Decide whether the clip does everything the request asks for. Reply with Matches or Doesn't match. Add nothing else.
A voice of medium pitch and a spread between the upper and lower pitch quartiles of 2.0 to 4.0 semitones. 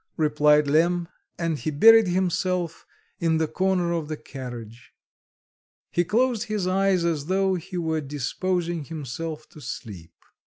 Matches